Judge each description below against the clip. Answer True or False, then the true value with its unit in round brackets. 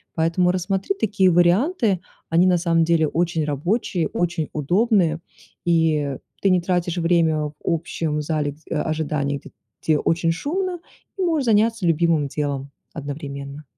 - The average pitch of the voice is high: False (165 Hz)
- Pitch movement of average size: True (3.3 semitones)